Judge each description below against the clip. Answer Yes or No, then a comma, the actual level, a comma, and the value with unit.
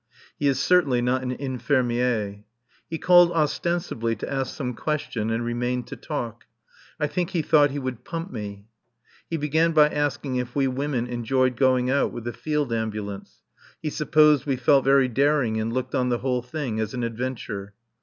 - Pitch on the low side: Yes, low, 130 Hz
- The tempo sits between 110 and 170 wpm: No, average, 180 wpm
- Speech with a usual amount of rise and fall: Yes, average, 3.8 semitones